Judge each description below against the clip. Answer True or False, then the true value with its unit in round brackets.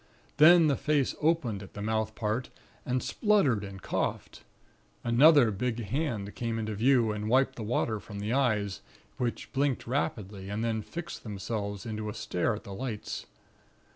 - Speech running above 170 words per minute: False (165 wpm)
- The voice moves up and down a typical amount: True (4.2 semitones)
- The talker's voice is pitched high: False (115 Hz)